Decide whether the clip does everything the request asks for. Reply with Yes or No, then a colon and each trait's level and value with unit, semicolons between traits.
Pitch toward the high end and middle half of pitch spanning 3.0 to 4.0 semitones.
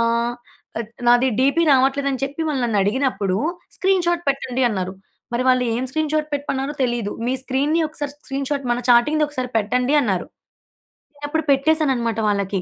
Yes: very high, 265 Hz; average, 3.5 semitones